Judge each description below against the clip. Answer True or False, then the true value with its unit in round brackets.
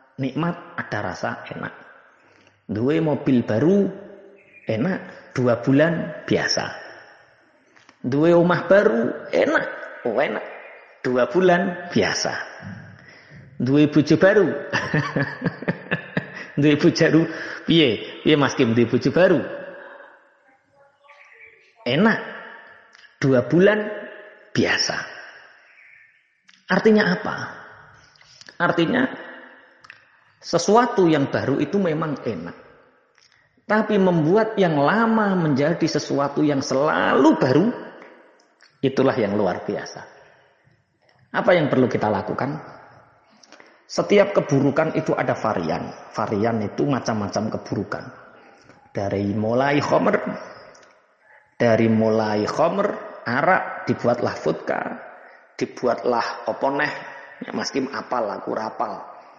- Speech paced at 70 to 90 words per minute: True (85 wpm)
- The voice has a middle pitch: True (160 Hz)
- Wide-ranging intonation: True (6.8 semitones)